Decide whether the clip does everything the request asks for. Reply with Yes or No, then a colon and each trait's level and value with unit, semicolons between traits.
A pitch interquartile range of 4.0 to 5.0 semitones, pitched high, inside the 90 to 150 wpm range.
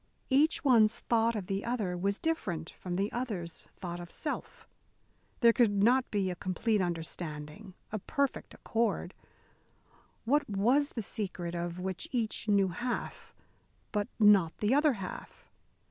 Yes: average, 4.7 semitones; high, 205 Hz; average, 145 wpm